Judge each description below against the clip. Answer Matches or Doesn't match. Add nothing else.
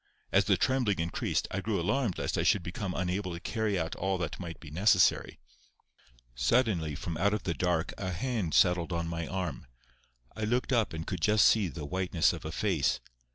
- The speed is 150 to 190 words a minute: Doesn't match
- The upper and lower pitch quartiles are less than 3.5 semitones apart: Doesn't match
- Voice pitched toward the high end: Doesn't match